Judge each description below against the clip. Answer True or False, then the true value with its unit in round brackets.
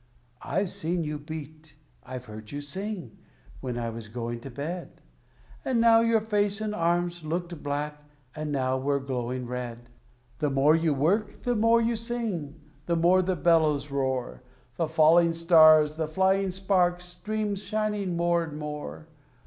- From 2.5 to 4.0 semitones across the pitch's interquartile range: False (5.0 semitones)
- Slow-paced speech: False (155 wpm)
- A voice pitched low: False (160 Hz)